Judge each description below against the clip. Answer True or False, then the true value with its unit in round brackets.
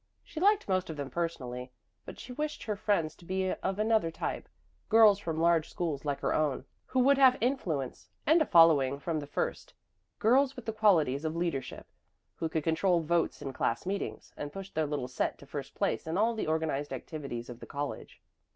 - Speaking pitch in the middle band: True (165 Hz)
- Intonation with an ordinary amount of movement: False (6.4 semitones)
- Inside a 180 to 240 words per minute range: True (200 wpm)